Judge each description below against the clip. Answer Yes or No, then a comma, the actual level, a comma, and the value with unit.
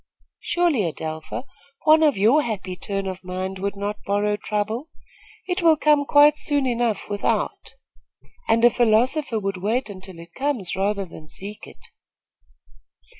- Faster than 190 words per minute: No, average, 145 wpm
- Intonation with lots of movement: Yes, wide, 6.3 semitones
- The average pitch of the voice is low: No, high, 210 Hz